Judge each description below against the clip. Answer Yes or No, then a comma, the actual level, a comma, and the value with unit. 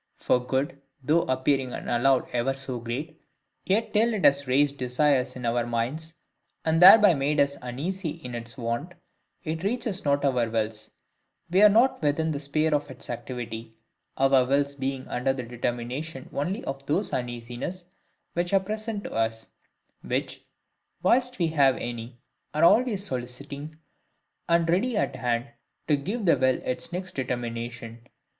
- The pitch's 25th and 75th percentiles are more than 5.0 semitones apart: Yes, wide, 5.4 semitones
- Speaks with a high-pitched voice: No, medium, 140 Hz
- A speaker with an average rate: Yes, average, 155 wpm